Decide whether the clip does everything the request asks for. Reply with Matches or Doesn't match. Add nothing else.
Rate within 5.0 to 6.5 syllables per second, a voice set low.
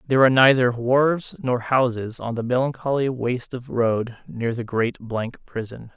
Doesn't match